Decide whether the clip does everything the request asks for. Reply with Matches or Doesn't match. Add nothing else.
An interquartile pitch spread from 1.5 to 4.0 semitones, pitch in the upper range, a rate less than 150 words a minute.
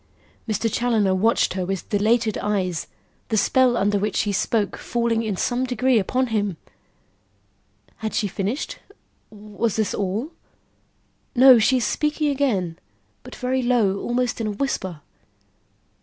Matches